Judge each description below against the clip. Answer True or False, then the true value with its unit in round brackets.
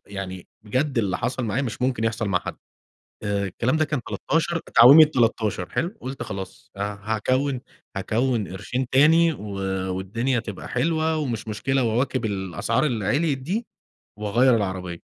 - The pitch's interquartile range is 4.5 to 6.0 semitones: True (4.9 semitones)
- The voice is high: False (120 Hz)